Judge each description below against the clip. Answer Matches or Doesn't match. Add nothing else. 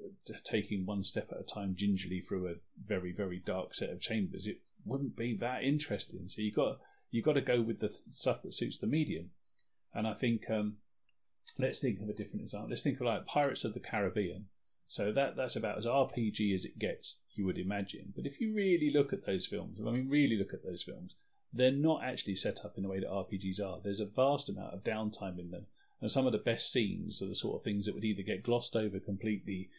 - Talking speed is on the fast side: Matches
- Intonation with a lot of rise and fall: Doesn't match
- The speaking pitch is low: Matches